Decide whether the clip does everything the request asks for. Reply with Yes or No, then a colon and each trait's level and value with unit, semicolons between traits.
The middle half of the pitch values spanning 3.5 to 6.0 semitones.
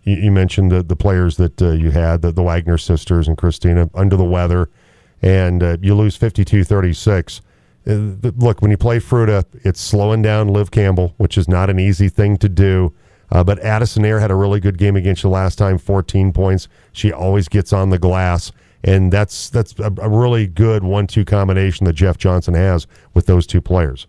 No: narrow, 2.5 semitones